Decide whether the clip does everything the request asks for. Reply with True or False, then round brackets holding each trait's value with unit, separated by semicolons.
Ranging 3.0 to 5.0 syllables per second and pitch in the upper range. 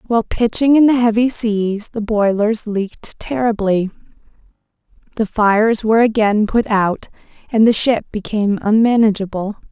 True (4.8 syllables/s; 215 Hz)